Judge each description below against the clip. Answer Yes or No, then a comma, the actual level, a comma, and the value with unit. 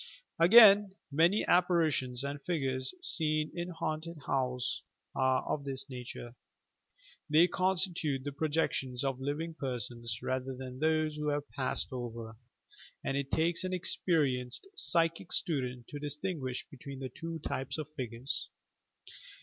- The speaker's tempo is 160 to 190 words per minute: No, slow, 135 wpm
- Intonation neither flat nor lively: Yes, average, 4.2 semitones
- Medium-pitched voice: Yes, medium, 145 Hz